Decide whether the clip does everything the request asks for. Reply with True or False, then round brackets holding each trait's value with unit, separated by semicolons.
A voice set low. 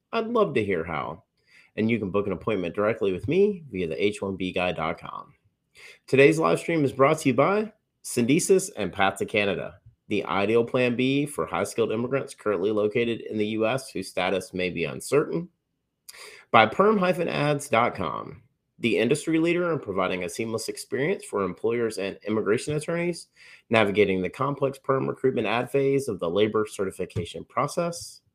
True (130 Hz)